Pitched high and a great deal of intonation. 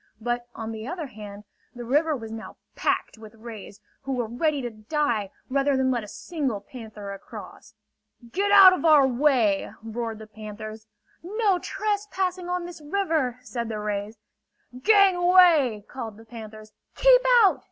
Yes: high, 245 Hz; wide, 7.5 semitones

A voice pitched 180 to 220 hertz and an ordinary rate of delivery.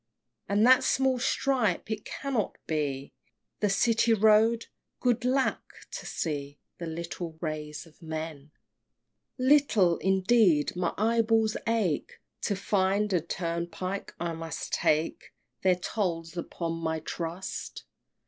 No: medium, 185 Hz; slow, 120 wpm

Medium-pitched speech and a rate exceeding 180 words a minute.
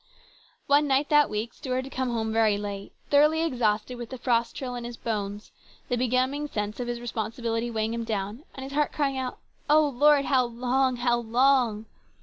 No: high, 245 Hz; average, 195 wpm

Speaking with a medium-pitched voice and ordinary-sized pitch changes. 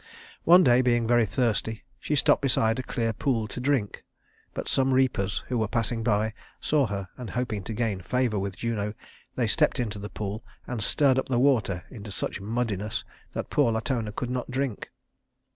No: low, 115 Hz; average, 3.1 semitones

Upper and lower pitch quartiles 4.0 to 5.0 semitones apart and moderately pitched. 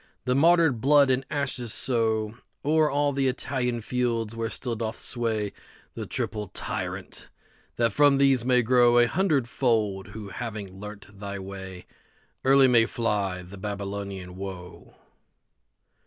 No: average, 4.4 semitones; low, 115 Hz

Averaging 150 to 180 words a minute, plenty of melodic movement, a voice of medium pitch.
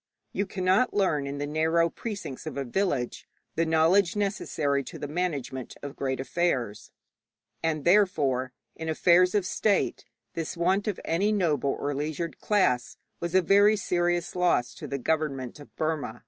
No: average, 160 wpm; average, 4.7 semitones; medium, 160 Hz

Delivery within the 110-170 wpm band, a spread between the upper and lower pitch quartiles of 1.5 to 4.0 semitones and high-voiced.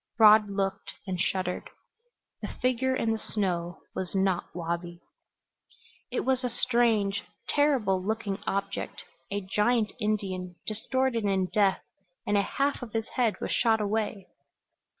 Yes: slow, 135 wpm; average, 3.2 semitones; high, 210 Hz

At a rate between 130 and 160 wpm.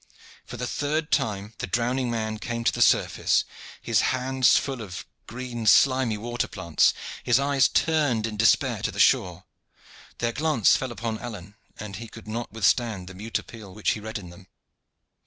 No: average, 175 wpm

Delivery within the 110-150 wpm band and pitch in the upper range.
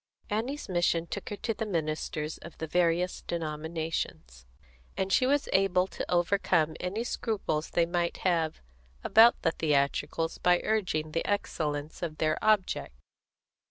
No: average, 140 wpm; medium, 170 Hz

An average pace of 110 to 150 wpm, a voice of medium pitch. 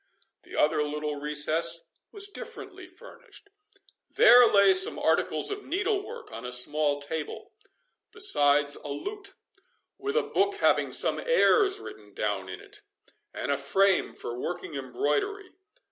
Yes: average, 140 wpm; medium, 170 Hz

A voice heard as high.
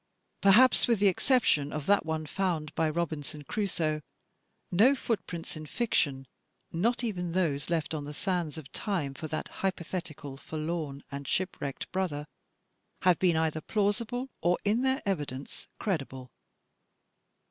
No: medium, 165 Hz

